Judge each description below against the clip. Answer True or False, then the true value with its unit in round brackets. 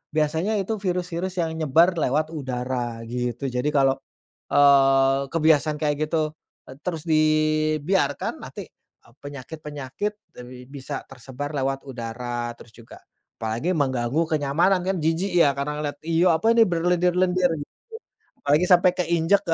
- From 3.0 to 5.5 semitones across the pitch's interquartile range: True (4.1 semitones)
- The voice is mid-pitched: True (150 Hz)